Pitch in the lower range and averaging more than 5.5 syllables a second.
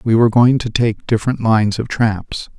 No: low, 115 Hz; 5.4 syllables/s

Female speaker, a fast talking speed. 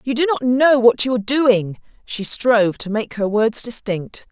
Yes: female; fast, 210 wpm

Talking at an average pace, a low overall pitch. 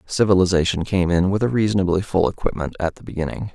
Yes: average, 185 wpm; very low, 95 Hz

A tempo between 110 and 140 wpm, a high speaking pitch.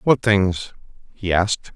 No: slow, 135 wpm; low, 100 Hz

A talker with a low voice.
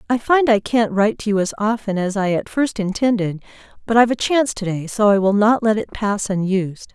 No: high, 210 Hz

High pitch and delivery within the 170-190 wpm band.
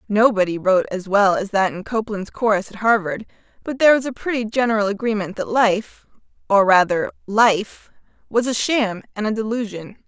No: high, 210 Hz; average, 160 wpm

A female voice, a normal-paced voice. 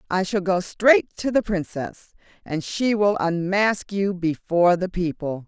Yes: female; average, 165 wpm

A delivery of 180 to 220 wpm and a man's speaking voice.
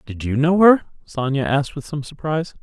Yes: fast, 205 wpm; male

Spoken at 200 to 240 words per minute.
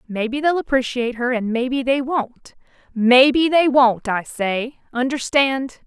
No: average, 145 wpm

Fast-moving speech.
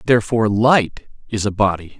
No: average, 150 wpm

